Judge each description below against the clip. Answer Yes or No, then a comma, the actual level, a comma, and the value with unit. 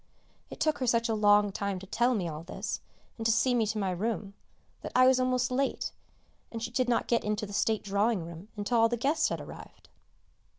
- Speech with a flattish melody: No, average, 3.4 semitones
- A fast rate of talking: Yes, fast, 225 wpm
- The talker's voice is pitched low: No, high, 225 Hz